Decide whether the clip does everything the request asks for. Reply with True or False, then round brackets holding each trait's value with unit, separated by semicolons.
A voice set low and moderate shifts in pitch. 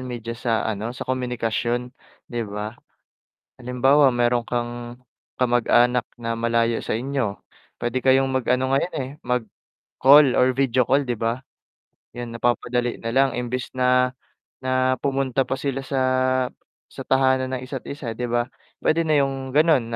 False (125 Hz; 1.8 semitones)